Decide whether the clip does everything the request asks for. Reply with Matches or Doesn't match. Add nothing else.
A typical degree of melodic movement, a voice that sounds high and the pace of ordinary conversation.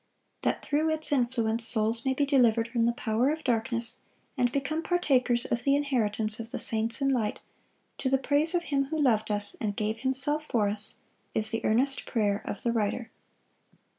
Matches